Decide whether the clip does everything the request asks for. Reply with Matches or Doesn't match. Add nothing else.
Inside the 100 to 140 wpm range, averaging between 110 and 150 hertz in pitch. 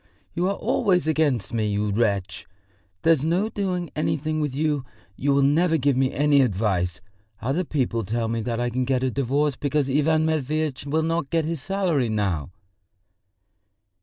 Doesn't match